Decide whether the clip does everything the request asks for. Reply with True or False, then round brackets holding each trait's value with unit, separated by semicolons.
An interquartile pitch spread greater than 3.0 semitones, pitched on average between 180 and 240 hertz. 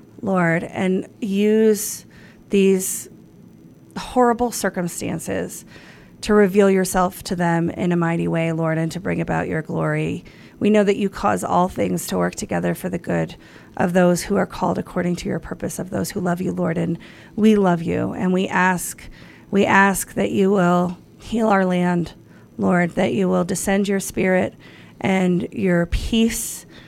False (2.6 semitones; 185 Hz)